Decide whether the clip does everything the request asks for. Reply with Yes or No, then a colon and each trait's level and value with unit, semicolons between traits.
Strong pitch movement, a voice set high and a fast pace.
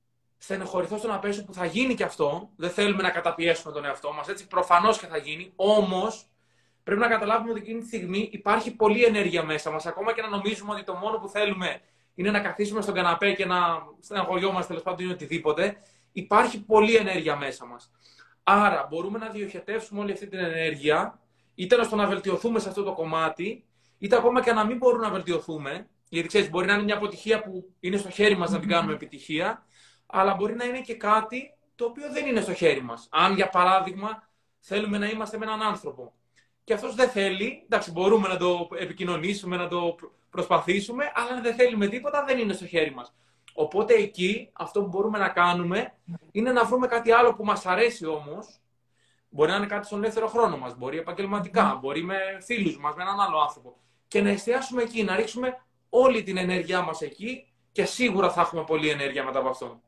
No: average, 4.2 semitones; high, 195 Hz; fast, 200 wpm